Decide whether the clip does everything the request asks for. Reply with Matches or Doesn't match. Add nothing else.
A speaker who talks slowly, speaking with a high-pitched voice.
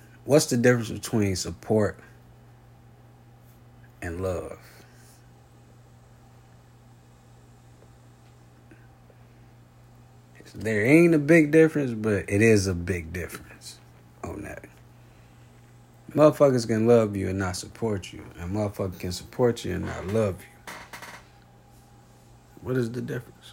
Doesn't match